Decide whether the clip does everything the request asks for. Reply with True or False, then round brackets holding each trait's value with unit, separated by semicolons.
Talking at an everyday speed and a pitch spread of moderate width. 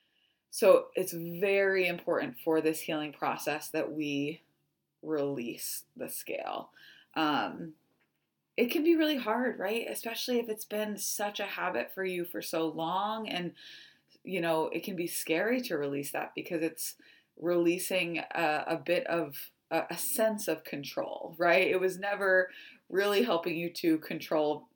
True (155 wpm; 4.2 semitones)